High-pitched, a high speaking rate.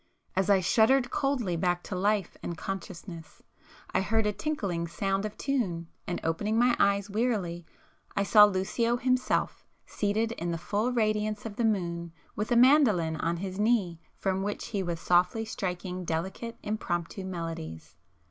No: high, 195 Hz; average, 165 wpm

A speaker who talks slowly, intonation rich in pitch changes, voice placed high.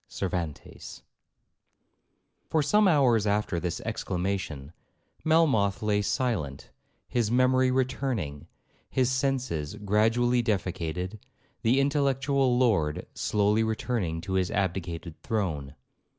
No: slow, 90 wpm; wide, 6.1 semitones; low, 105 Hz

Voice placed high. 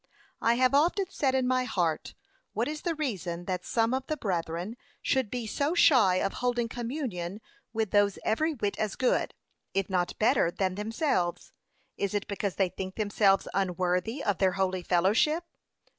Yes: high, 210 Hz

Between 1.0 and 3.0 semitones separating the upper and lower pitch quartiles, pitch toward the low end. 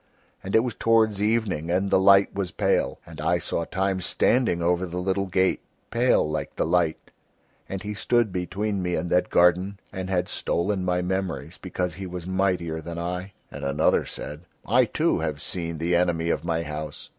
Yes: narrow, 2.4 semitones; very low, 90 Hz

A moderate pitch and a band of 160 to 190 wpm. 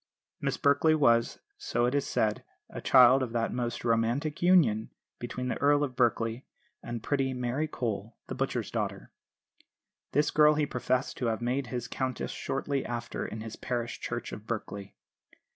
No: low, 125 Hz; average, 165 wpm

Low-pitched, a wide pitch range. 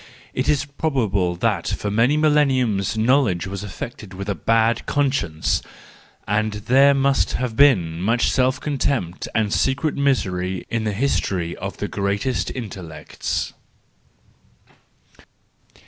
Yes: low, 110 Hz; wide, 5.7 semitones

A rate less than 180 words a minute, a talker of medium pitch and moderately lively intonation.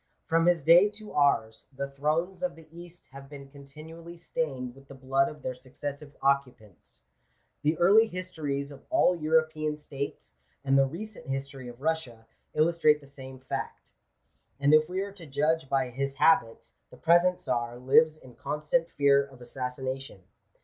Yes: average, 165 wpm; medium, 145 Hz; average, 3.4 semitones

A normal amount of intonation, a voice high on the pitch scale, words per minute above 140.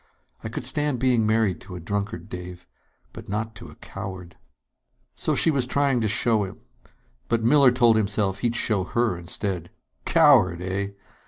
No: average, 4.3 semitones; low, 105 Hz; average, 170 wpm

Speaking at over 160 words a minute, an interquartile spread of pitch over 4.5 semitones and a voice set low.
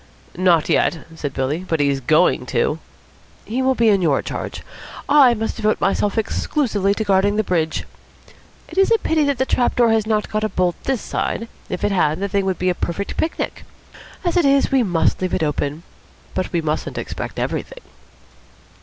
No: average, 190 wpm; wide, 5.5 semitones; high, 200 Hz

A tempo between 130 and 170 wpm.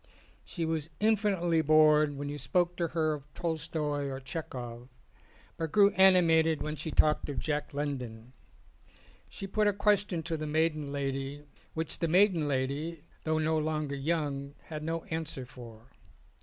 Yes: average, 155 wpm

